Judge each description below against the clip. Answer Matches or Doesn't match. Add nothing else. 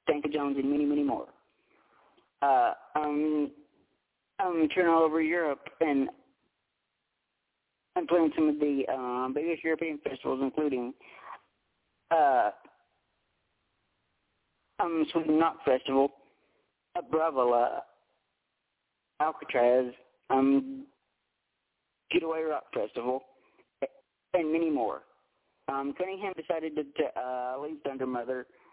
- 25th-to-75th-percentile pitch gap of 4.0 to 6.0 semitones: Doesn't match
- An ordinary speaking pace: Doesn't match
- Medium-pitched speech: Matches